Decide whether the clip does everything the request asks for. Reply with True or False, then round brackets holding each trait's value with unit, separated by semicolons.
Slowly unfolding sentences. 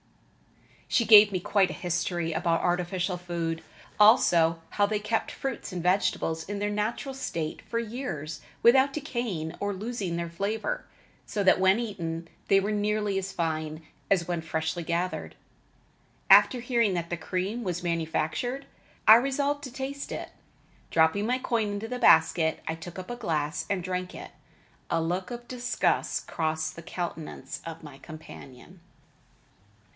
False (155 wpm)